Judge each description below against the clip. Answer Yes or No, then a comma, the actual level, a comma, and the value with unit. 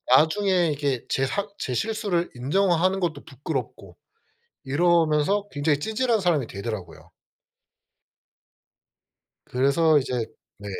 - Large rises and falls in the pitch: Yes, wide, 5.9 semitones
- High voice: No, medium, 155 Hz